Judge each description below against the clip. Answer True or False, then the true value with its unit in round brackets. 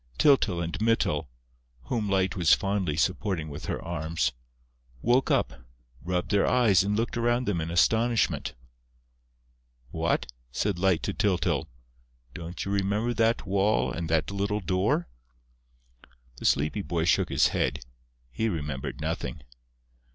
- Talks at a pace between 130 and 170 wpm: True (135 wpm)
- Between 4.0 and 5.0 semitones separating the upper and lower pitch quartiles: True (4.3 semitones)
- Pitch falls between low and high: False (95 Hz)